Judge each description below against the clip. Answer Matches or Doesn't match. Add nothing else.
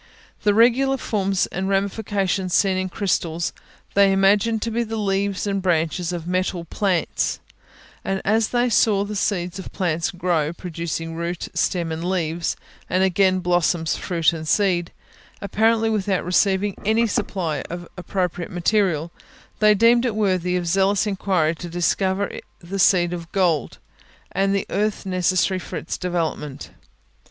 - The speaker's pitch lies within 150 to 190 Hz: Matches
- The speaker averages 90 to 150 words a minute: Matches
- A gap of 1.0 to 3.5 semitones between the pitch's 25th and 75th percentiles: Matches